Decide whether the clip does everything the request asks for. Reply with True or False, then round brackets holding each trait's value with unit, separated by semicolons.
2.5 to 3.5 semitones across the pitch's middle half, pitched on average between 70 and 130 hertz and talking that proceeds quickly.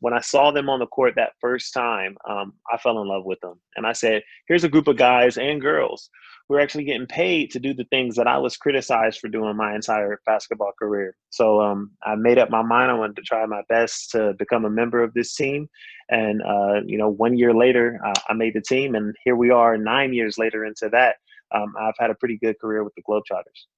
True (2.8 semitones; 115 Hz; 245 wpm)